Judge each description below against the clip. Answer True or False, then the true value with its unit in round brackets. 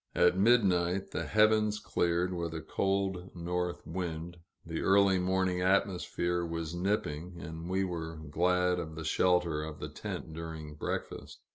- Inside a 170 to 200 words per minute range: False (145 wpm)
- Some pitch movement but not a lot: False (2.3 semitones)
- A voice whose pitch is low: True (90 Hz)